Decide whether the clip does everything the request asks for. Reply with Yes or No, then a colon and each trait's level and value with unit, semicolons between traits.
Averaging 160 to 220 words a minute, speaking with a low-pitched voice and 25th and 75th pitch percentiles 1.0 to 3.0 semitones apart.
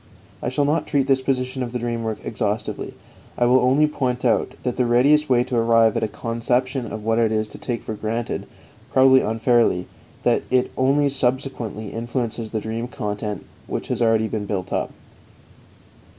Yes: average, 180 wpm; low, 120 Hz; average, 2.7 semitones